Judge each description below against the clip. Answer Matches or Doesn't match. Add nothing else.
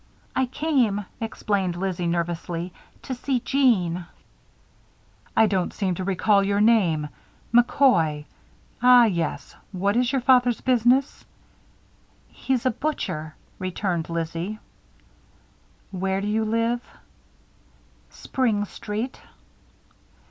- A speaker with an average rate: Doesn't match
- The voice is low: Doesn't match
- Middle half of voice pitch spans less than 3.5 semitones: Doesn't match